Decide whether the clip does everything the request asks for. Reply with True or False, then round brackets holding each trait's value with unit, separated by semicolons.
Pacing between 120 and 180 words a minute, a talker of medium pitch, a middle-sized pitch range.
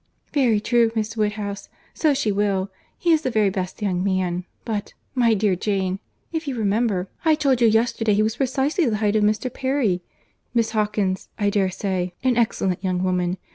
False (175 wpm; 210 Hz; 3.8 semitones)